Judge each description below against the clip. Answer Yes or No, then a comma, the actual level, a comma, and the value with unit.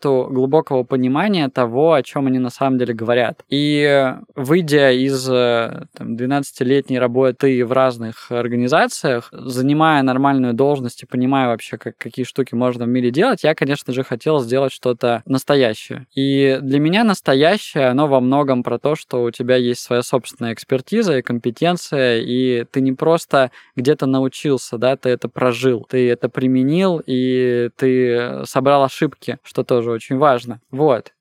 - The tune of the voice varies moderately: No, narrow, 2.2 semitones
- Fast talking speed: No, average, 150 wpm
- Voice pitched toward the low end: Yes, low, 130 Hz